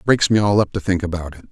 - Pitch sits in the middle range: No, very low, 95 Hz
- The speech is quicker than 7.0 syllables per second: Yes, 7.2 syllables/s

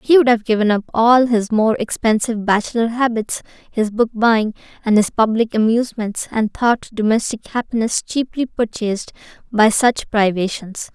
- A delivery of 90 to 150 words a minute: Yes, average, 145 wpm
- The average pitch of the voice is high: Yes, high, 225 Hz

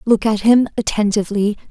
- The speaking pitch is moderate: No, high, 215 Hz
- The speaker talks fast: No, average, 140 wpm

